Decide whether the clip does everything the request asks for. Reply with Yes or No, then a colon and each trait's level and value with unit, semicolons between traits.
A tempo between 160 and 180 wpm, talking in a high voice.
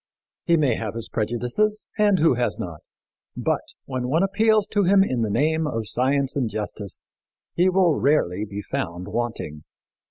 No: average, 165 wpm; low, 130 Hz